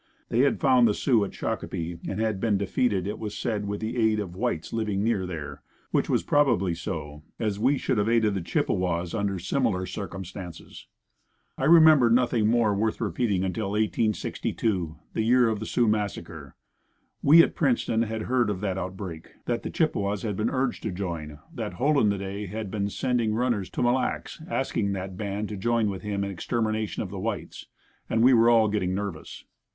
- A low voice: Yes, low, 105 Hz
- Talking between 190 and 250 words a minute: Yes, average, 195 wpm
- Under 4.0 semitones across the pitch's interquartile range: Yes, average, 3.4 semitones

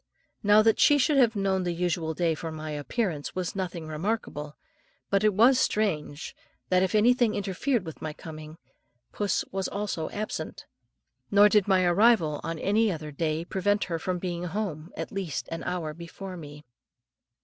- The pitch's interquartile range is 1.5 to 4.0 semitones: No, average, 4.5 semitones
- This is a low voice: No, medium, 180 Hz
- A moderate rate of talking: Yes, average, 170 wpm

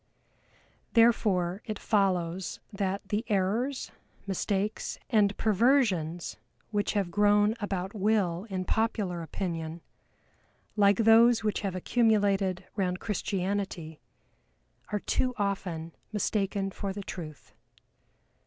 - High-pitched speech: Yes, high, 200 Hz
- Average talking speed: No, slow, 100 wpm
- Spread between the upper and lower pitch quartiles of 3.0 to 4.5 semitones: No, narrow, 2.6 semitones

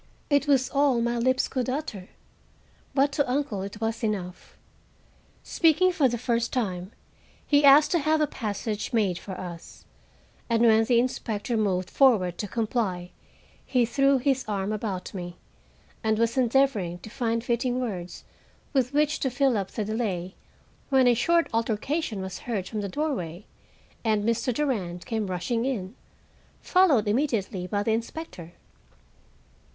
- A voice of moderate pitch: No, high, 230 Hz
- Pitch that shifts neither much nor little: Yes, average, 4.9 semitones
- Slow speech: No, average, 150 wpm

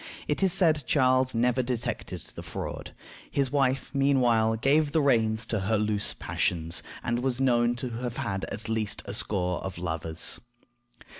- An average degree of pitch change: Yes, average, 3.8 semitones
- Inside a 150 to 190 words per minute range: Yes, average, 160 wpm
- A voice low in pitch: Yes, low, 120 Hz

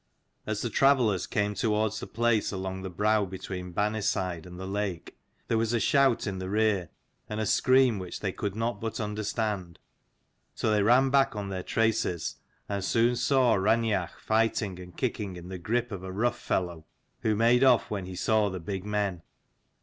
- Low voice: Yes, low, 105 Hz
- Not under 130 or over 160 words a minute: No, average, 185 wpm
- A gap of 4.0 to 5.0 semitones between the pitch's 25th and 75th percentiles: No, average, 3.2 semitones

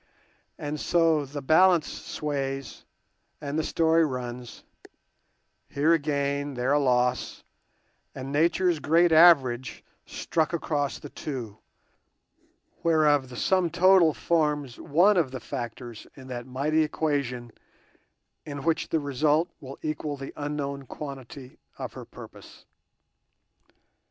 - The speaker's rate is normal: No, slow, 115 wpm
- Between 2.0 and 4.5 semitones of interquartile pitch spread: Yes, average, 3.2 semitones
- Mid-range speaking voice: Yes, medium, 145 Hz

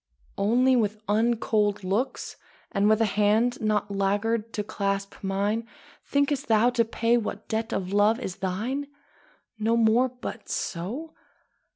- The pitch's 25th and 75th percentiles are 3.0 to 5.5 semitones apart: No, narrow, 2.6 semitones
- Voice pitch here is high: Yes, high, 220 Hz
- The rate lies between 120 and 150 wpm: Yes, average, 140 wpm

